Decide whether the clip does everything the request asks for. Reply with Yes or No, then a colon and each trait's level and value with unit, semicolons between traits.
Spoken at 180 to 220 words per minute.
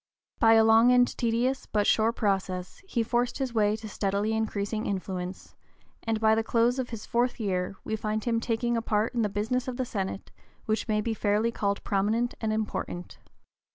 Yes: average, 190 wpm